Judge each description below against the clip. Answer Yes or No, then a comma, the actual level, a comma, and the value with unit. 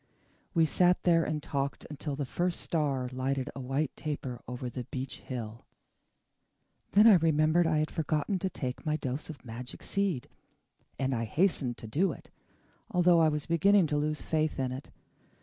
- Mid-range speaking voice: Yes, medium, 150 Hz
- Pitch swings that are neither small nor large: Yes, average, 4.1 semitones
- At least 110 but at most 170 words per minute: No, average, 180 wpm